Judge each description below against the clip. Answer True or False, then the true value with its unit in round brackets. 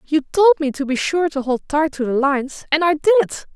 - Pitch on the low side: False (300 Hz)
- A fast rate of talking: True (255 wpm)